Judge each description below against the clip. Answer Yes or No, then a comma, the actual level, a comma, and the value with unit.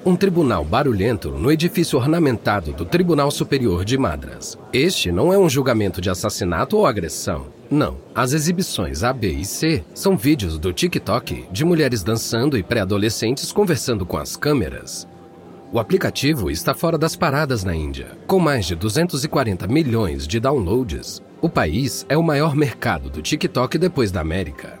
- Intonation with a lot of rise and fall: Yes, wide, 9.0 semitones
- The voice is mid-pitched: No, low, 125 Hz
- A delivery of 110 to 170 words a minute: Yes, average, 160 wpm